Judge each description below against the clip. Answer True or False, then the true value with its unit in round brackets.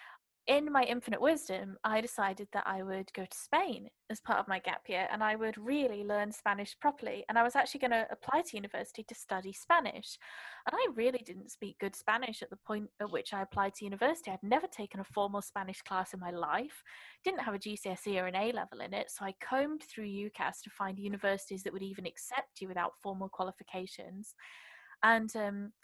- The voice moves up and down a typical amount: True (3.6 semitones)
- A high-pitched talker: True (210 Hz)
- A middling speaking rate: False (210 wpm)